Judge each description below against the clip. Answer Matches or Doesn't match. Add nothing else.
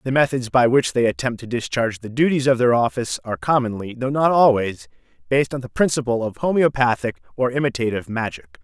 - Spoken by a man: Matches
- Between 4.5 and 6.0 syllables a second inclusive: Doesn't match